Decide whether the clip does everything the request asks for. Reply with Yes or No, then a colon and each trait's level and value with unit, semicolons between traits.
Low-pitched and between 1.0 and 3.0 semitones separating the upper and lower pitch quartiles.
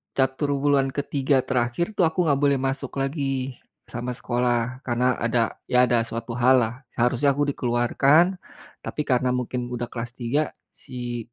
Yes: low, 130 Hz; narrow, 2.4 semitones